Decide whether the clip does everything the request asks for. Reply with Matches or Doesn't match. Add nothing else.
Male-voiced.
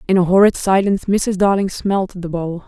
Doesn't match